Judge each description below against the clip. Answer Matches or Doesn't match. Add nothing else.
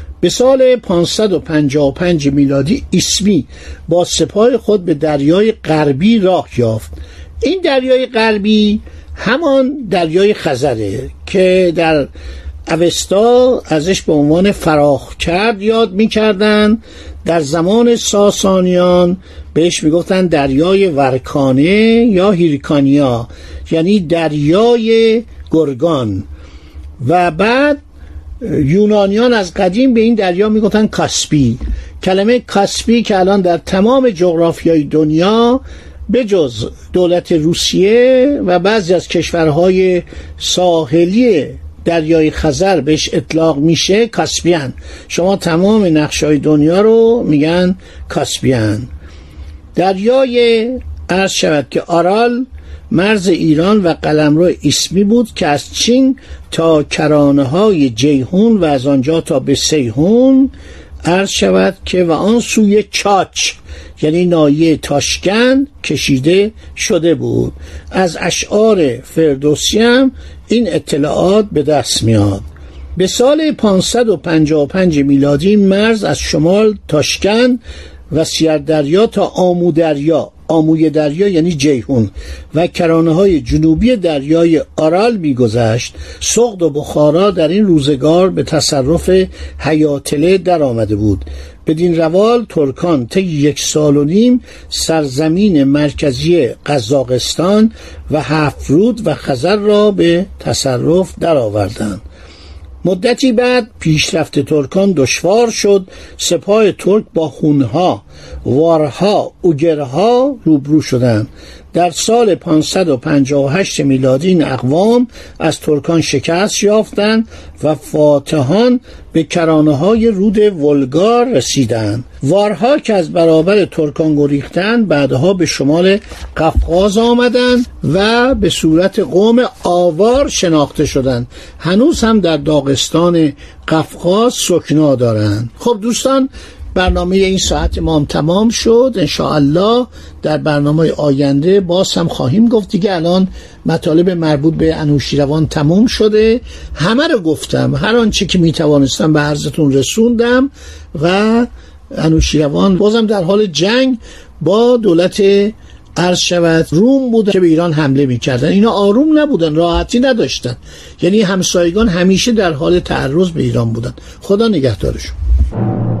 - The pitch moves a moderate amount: Doesn't match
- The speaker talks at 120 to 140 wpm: Doesn't match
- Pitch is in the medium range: Matches